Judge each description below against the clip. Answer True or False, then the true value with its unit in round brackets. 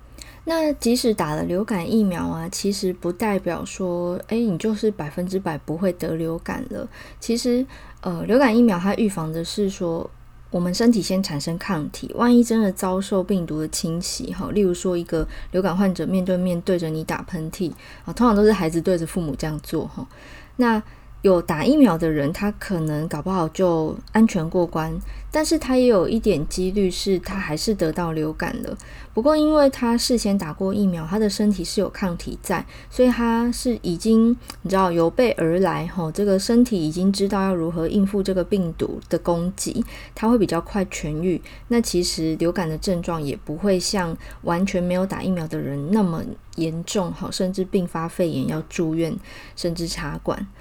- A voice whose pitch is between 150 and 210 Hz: True (185 Hz)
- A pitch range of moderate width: True (3.9 semitones)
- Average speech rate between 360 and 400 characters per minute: False (280 characters per minute)